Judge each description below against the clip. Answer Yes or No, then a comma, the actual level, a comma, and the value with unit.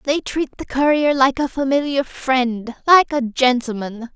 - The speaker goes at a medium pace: Yes, average, 145 wpm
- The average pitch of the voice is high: Yes, very high, 265 Hz